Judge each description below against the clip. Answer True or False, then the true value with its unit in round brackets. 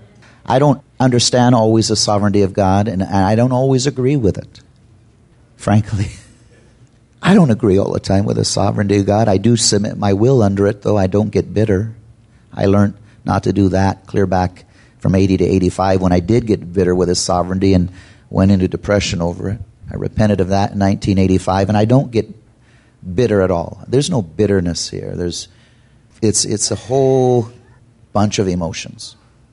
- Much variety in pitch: False (3.5 semitones)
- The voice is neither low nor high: False (105 Hz)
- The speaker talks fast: False (185 wpm)